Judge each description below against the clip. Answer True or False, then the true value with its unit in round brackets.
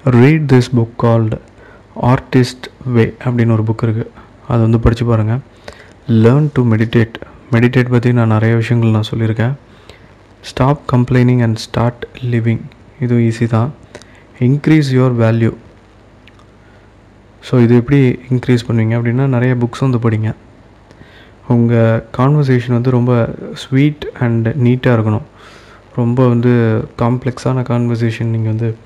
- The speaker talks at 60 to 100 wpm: False (125 wpm)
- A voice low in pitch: True (120 Hz)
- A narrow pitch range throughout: True (1.8 semitones)